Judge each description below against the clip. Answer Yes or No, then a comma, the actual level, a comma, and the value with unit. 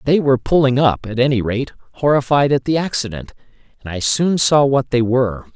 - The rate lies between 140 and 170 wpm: No, average, 195 wpm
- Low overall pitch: Yes, low, 130 Hz